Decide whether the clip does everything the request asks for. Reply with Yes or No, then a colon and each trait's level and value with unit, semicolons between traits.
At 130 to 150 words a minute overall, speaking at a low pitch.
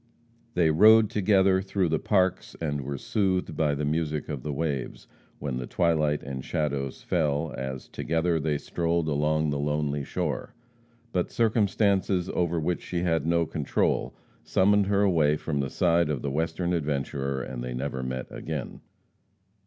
No: average, 160 wpm; very low, 80 Hz